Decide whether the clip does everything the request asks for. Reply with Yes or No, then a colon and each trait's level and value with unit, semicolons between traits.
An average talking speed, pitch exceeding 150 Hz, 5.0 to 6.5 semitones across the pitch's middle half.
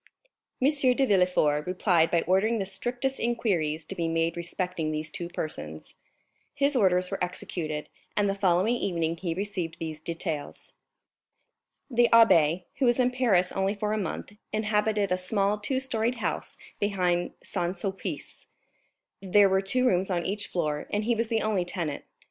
No: average, 160 wpm; high, 190 Hz; average, 4.2 semitones